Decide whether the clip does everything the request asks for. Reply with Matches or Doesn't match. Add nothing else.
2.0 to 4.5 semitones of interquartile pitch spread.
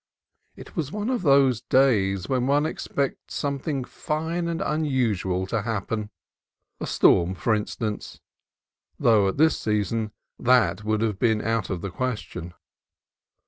Doesn't match